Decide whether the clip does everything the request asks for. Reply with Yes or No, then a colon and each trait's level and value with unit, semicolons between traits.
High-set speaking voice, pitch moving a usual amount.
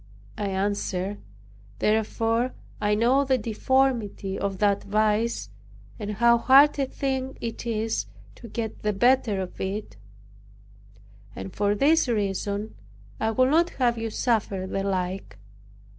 Yes: high, 215 Hz; average, 3.4 semitones